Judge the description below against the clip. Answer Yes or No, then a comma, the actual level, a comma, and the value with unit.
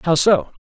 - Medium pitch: Yes, medium, 170 Hz